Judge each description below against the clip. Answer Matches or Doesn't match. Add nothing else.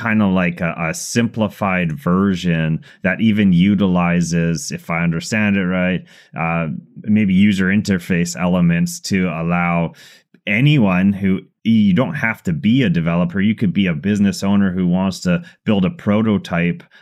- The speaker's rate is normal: Matches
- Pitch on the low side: Matches